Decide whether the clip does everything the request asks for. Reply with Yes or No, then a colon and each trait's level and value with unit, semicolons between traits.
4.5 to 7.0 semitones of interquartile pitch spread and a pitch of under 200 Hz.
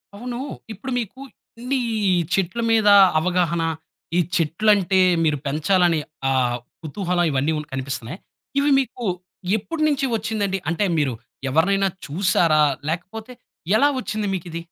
Yes: average, 5.2 semitones; high, 190 Hz